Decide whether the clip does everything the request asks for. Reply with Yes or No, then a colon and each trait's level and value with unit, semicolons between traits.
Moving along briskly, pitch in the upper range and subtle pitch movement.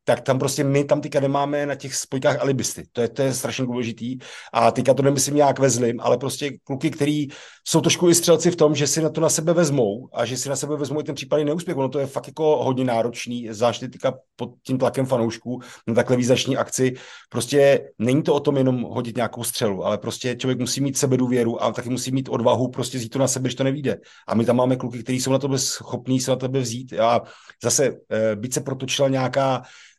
No: fast, 235 wpm; low, 130 Hz; narrow, 2.3 semitones